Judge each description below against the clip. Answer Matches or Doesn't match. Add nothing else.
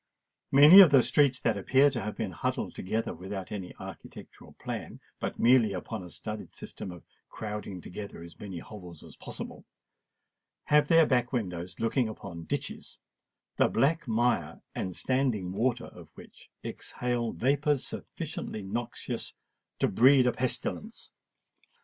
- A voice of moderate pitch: Doesn't match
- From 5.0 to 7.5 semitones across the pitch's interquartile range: Matches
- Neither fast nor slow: Matches